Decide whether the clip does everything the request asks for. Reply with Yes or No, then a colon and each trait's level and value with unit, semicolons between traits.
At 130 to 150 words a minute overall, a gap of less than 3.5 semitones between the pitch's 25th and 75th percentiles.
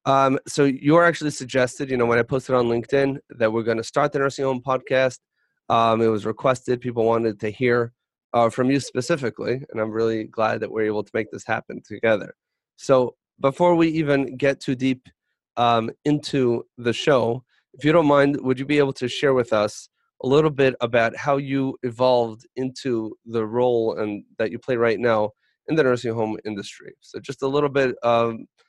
No: average, 200 wpm; average, 3.1 semitones